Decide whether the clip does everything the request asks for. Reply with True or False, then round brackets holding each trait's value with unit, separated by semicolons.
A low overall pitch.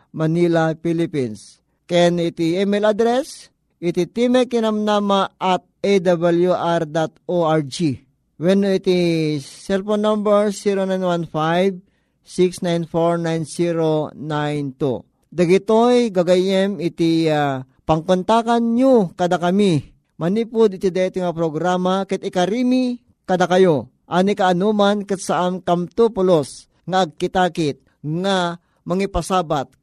False (180 Hz)